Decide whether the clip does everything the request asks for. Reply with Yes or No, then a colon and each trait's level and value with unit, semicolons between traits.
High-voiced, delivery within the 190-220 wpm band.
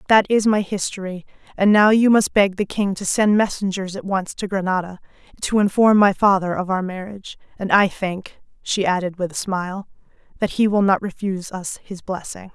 Yes: high, 195 Hz; average, 195 wpm